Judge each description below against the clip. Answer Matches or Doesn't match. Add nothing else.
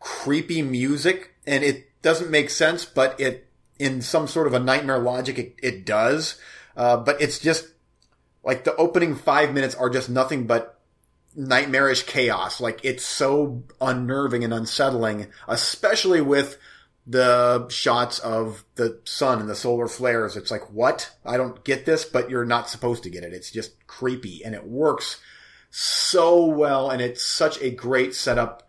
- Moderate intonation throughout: Matches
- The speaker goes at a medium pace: Matches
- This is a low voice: Matches